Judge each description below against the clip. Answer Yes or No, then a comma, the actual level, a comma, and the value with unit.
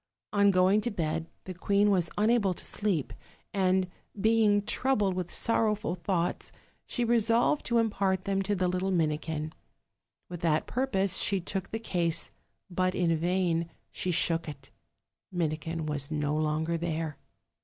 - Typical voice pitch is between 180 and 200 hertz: Yes, medium, 185 Hz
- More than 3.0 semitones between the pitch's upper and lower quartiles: Yes, average, 3.7 semitones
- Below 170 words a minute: Yes, average, 150 wpm